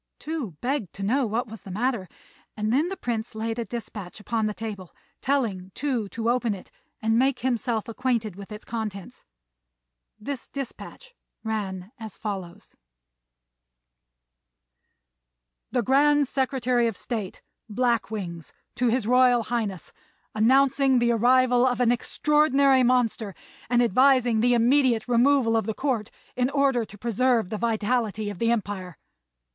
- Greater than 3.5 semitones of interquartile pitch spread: No, average, 3.2 semitones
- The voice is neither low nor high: No, high, 235 Hz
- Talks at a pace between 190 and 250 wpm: No, average, 140 wpm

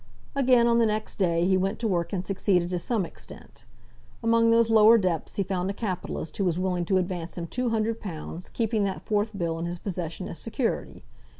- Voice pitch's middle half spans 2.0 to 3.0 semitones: No, average, 4.1 semitones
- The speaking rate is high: Yes, fast, 210 wpm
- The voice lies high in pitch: Yes, high, 195 Hz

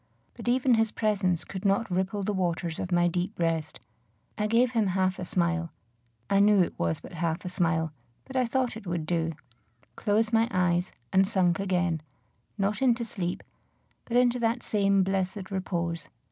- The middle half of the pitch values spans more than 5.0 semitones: No, average, 3.8 semitones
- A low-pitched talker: No, high, 190 Hz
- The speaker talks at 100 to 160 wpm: No, average, 175 wpm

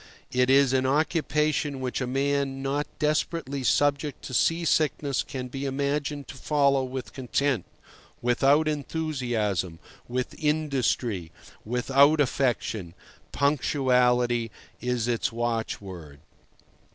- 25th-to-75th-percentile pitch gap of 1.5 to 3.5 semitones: Yes, average, 2.8 semitones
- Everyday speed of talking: No, slow, 105 wpm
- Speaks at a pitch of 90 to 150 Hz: Yes, low, 135 Hz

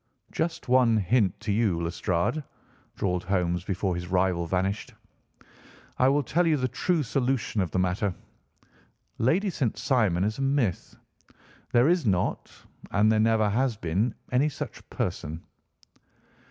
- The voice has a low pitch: Yes, low, 110 Hz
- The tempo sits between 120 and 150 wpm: Yes, average, 140 wpm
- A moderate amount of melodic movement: No, wide, 6.1 semitones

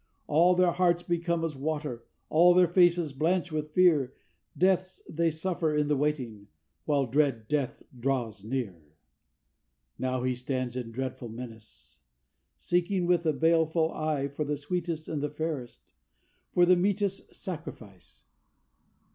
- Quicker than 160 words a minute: No, average, 140 wpm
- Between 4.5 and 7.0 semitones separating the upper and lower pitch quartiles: Yes, average, 5.1 semitones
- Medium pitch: Yes, medium, 150 Hz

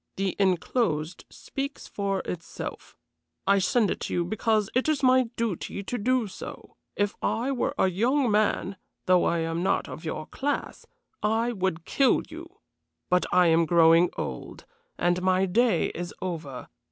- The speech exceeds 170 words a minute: No, average, 160 wpm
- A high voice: Yes, high, 195 Hz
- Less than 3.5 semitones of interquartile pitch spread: No, wide, 5.4 semitones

